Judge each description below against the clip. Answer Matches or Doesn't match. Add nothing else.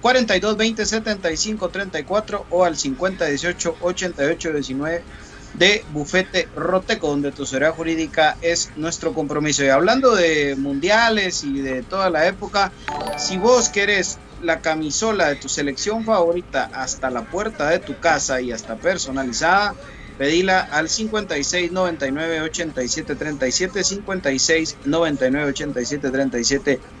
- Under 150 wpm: Matches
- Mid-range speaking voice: Matches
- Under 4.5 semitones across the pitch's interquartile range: Doesn't match